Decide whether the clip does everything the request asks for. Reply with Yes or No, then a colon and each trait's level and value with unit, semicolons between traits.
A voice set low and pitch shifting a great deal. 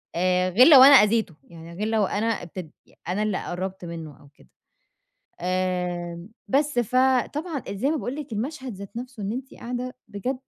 No: high, 210 Hz; wide, 5.9 semitones